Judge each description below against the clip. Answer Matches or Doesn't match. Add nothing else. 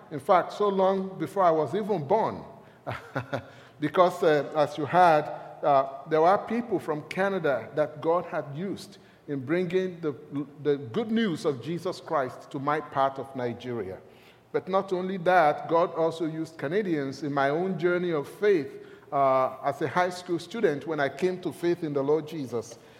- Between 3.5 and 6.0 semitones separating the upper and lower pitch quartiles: Matches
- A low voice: Doesn't match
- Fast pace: Doesn't match